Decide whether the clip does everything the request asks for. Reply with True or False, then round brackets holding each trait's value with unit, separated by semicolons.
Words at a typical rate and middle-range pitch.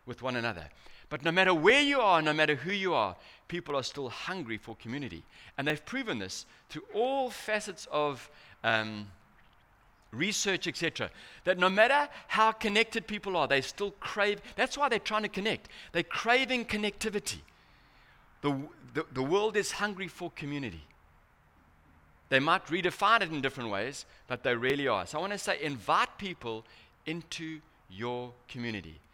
True (165 wpm; 155 Hz)